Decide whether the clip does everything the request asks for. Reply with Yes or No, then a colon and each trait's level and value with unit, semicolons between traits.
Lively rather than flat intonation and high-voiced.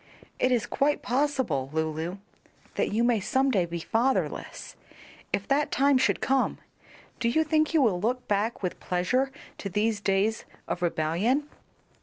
Yes: wide, 6.5 semitones; high, 225 Hz